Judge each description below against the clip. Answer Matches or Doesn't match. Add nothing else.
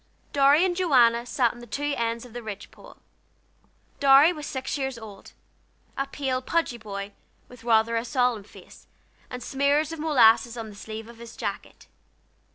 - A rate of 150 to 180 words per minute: Matches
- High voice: Matches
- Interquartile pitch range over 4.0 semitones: Doesn't match